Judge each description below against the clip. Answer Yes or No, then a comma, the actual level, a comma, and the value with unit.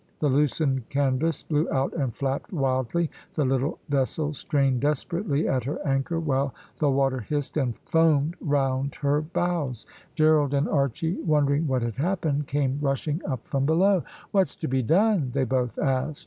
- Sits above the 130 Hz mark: Yes, medium, 140 Hz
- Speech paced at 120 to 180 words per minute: Yes, average, 160 wpm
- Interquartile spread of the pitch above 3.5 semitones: No, average, 2.8 semitones